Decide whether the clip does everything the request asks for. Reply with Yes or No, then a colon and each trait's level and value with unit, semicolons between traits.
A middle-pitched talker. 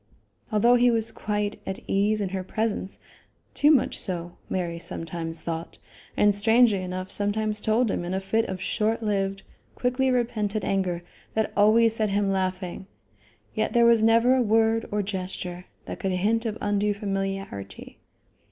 No: high, 205 Hz